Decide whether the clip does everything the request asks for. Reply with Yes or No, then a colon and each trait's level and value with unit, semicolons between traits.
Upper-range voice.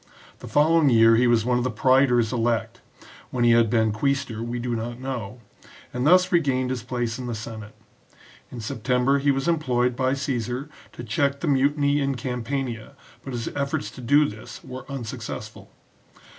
No: low, 125 Hz